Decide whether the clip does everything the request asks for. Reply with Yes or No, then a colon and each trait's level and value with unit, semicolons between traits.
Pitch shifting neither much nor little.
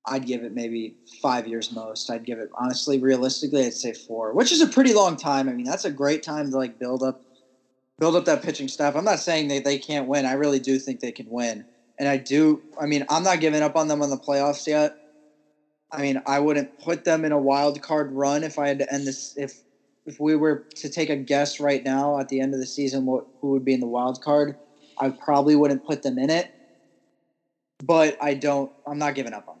No: narrow, 2.2 semitones